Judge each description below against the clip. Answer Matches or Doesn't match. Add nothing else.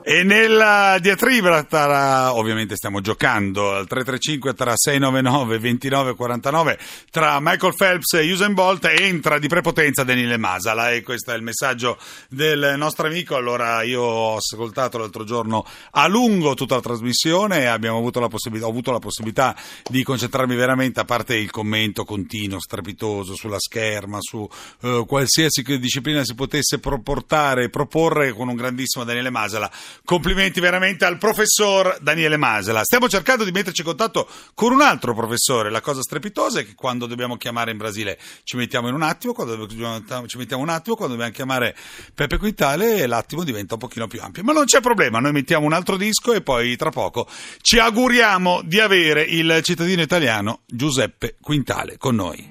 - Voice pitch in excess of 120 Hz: Matches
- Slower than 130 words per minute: Doesn't match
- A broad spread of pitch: Matches